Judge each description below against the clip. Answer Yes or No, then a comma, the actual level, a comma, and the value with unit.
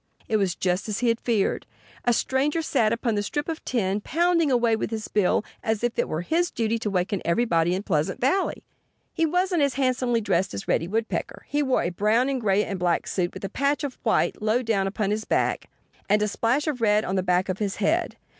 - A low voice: No, high, 220 Hz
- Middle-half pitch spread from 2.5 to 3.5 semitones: No, average, 5.1 semitones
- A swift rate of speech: Yes, fast, 230 wpm